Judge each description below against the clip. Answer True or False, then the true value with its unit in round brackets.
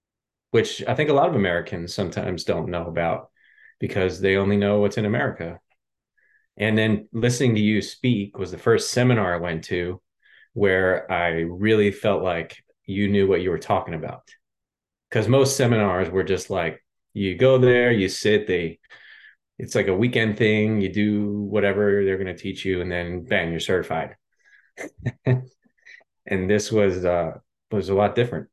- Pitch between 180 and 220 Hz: False (100 Hz)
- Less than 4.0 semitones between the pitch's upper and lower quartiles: True (2.9 semitones)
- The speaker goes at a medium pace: True (170 wpm)